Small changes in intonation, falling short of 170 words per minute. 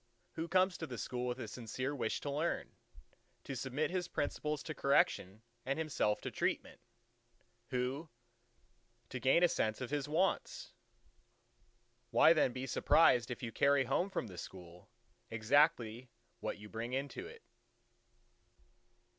No: average, 4.7 semitones; average, 145 wpm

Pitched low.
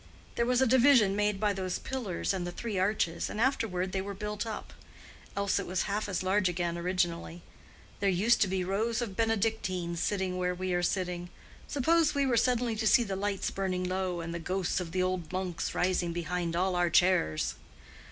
No: high, 190 Hz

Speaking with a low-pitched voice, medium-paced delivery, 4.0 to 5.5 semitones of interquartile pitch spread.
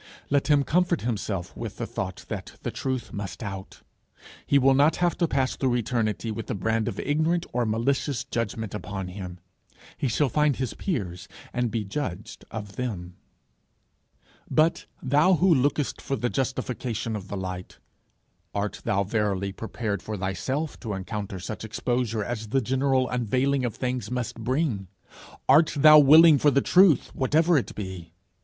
Yes: low, 120 Hz; average, 160 wpm; average, 5.2 semitones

